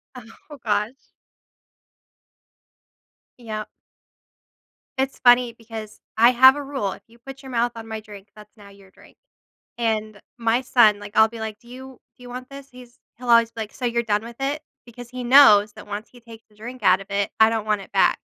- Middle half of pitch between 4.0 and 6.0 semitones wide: No, average, 2.7 semitones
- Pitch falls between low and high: No, high, 230 Hz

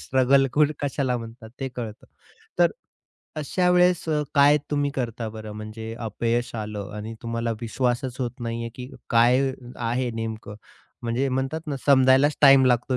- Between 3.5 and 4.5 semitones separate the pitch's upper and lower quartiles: No, average, 3.0 semitones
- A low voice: Yes, low, 125 Hz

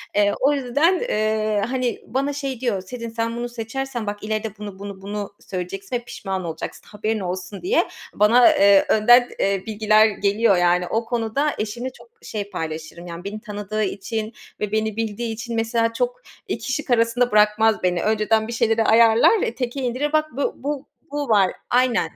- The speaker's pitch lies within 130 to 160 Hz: No, high, 220 Hz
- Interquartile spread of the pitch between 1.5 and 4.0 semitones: Yes, average, 3.0 semitones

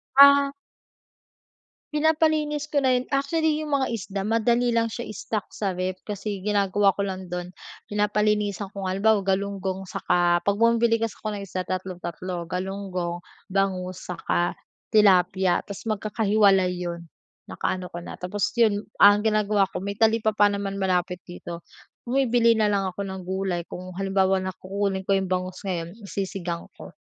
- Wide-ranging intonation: No, average, 2.8 semitones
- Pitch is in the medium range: No, high, 195 Hz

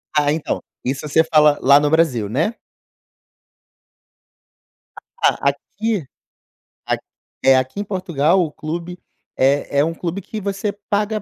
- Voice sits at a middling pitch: Yes, medium, 160 Hz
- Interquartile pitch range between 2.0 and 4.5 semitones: No, average, 5.1 semitones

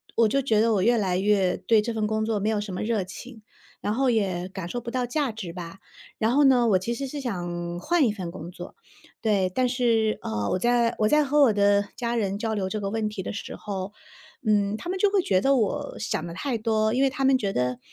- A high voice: Yes, high, 215 Hz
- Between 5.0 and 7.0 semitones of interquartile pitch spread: No, average, 4.0 semitones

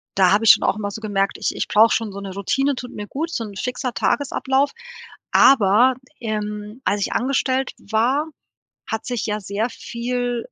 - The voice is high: Yes, high, 225 Hz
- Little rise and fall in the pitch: No, average, 3.6 semitones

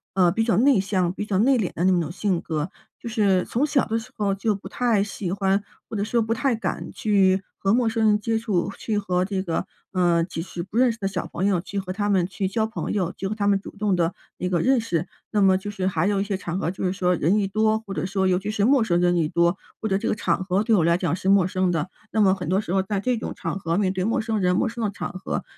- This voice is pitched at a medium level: No, high, 195 Hz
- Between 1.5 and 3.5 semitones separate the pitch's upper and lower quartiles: Yes, average, 2.9 semitones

